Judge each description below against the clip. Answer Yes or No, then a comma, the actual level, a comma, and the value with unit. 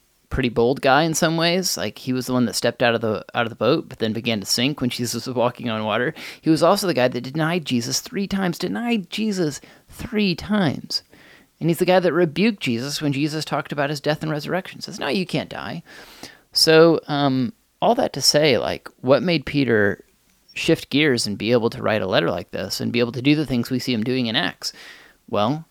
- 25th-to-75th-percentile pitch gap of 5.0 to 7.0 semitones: Yes, average, 5.3 semitones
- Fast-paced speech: Yes, fast, 235 wpm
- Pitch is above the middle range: No, medium, 140 Hz